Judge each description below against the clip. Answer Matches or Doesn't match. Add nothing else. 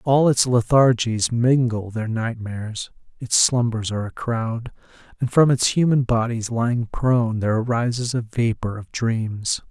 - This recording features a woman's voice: Doesn't match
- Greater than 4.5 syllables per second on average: Doesn't match